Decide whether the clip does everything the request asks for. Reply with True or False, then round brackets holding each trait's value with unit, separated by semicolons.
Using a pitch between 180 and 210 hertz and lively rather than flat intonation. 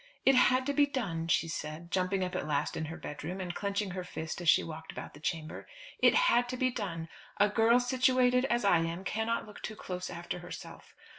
True (190 Hz; 6.6 semitones)